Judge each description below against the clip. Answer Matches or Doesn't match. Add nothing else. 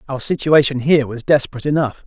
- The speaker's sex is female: Doesn't match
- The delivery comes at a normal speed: Matches